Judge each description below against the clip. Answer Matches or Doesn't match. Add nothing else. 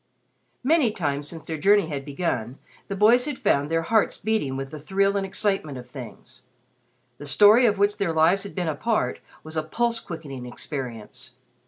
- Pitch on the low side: Doesn't match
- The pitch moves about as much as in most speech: Doesn't match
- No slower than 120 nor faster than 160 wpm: Doesn't match